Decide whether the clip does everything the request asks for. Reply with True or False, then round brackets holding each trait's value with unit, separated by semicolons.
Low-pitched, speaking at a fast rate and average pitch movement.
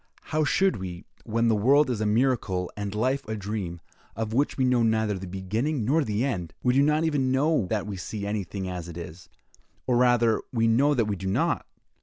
True (110 Hz; 215 wpm; 4.9 semitones)